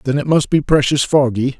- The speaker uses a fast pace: Yes, fast, 225 wpm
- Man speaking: Yes, male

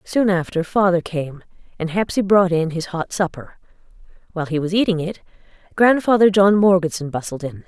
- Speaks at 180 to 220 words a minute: No, average, 165 wpm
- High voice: No, medium, 180 Hz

